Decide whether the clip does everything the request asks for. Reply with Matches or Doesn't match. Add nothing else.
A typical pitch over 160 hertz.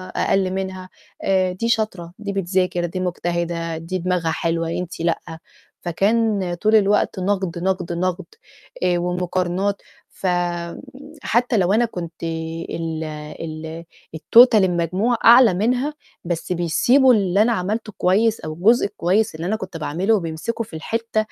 Matches